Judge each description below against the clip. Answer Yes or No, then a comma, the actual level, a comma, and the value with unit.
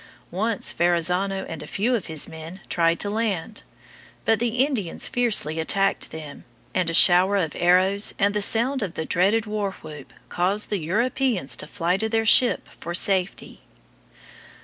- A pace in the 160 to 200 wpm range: Yes, average, 165 wpm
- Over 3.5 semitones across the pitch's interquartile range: Yes, average, 4.4 semitones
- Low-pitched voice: No, high, 195 Hz